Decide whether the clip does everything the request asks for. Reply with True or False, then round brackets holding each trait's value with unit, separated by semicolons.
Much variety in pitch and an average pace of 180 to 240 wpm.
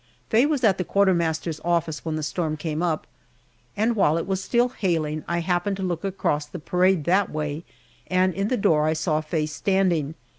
False (3.7 semitones; 195 wpm)